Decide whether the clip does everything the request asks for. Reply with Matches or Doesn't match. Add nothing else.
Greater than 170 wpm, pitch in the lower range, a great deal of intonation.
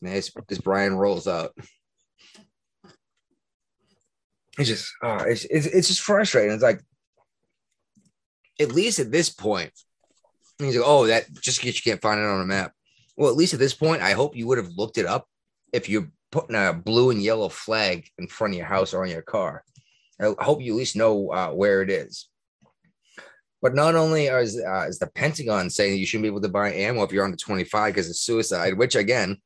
Matches